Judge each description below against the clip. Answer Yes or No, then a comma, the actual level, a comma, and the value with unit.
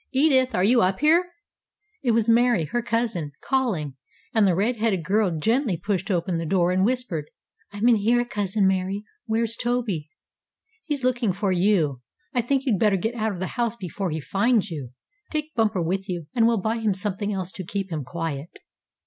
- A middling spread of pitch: Yes, average, 4.6 semitones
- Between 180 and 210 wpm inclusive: Yes, average, 190 wpm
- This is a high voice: Yes, high, 205 Hz